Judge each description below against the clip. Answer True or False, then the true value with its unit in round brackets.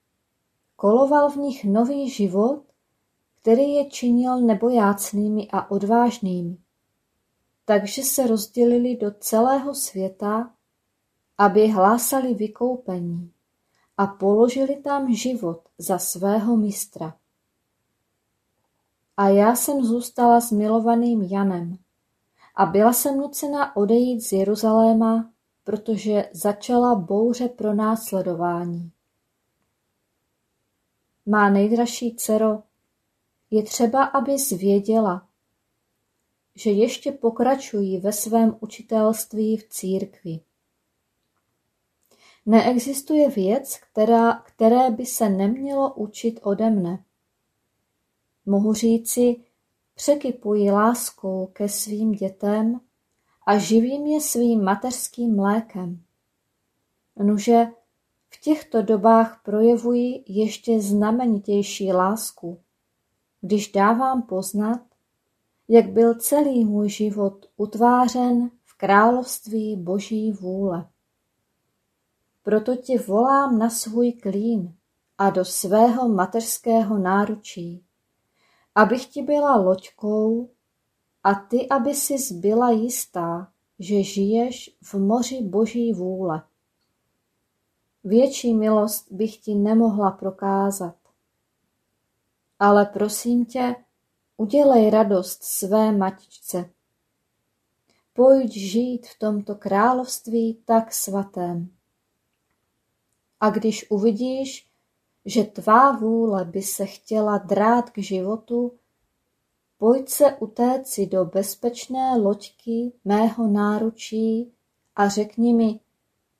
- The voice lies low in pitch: False (215 Hz)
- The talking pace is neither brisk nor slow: False (90 wpm)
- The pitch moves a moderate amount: True (3.3 semitones)